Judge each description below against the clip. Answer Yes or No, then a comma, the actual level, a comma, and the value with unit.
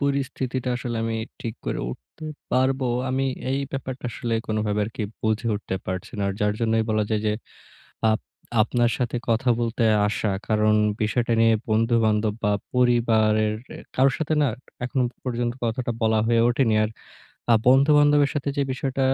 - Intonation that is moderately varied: Yes, average, 3.2 semitones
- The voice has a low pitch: Yes, low, 120 Hz